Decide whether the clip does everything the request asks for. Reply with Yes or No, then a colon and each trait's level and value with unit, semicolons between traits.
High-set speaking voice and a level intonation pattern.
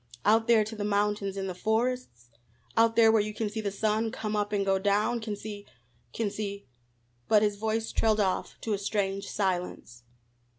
Yes: high, 210 Hz; narrow, 1.9 semitones